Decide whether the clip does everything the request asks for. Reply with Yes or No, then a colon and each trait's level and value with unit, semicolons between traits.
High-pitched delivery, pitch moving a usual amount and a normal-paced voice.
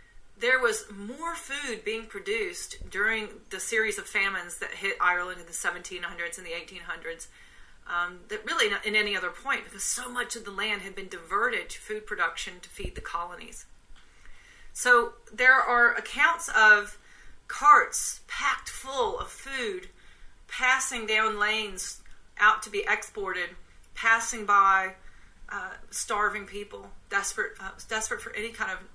Yes: high, 215 Hz; average, 4.2 semitones; average, 150 wpm